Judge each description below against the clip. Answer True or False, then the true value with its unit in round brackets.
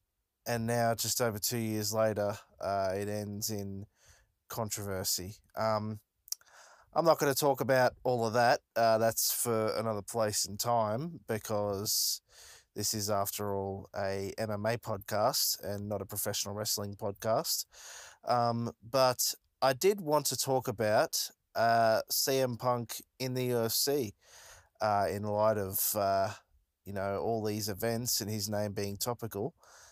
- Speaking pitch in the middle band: False (110 Hz)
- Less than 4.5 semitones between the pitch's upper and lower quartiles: True (2.7 semitones)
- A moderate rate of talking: True (145 wpm)